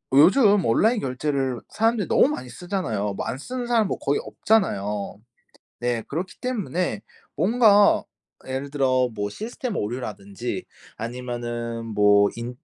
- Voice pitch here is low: Yes, low, 130 Hz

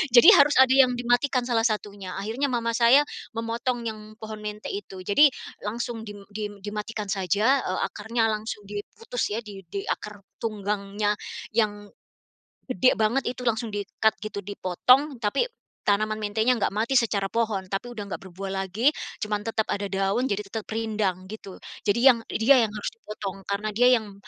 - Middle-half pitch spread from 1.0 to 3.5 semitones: Yes, average, 2.7 semitones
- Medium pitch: No, high, 215 Hz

